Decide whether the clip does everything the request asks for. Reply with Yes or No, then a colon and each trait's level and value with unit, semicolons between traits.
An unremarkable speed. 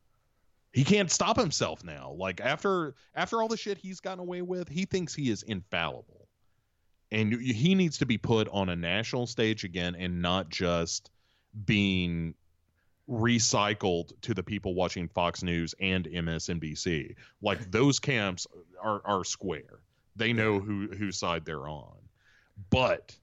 Yes: average, 150 wpm